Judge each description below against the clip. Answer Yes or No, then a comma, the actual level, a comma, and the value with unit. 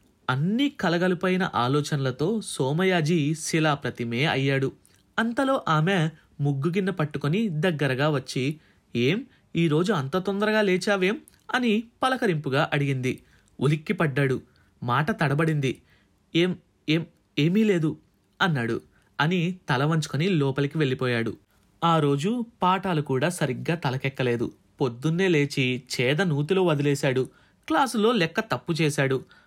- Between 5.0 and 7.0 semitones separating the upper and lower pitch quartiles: Yes, average, 5.3 semitones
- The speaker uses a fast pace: No, average, 100 wpm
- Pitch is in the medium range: Yes, medium, 155 Hz